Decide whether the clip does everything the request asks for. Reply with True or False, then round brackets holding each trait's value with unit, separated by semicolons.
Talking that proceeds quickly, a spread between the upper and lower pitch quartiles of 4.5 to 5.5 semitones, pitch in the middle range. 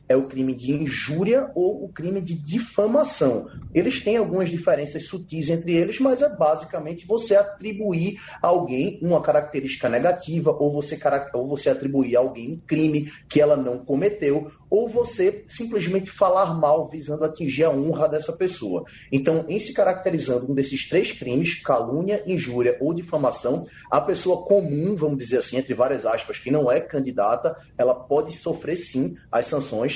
False (165 wpm; 5.2 semitones; 155 Hz)